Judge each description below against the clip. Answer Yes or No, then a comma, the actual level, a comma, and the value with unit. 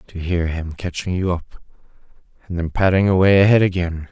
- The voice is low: Yes, very low, 90 Hz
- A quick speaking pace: No, average, 175 wpm